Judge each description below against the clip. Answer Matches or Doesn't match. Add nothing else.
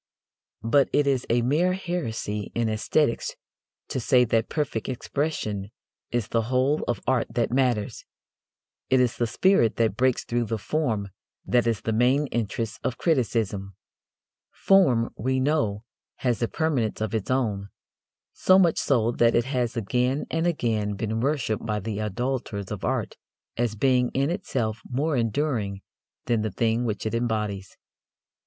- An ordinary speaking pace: Matches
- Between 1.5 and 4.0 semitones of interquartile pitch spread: Matches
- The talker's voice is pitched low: Matches